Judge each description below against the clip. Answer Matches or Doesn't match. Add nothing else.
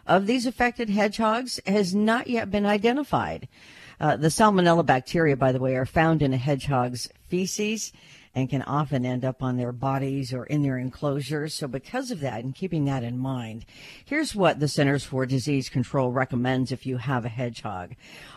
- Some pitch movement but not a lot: Doesn't match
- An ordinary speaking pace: Matches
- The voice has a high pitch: Doesn't match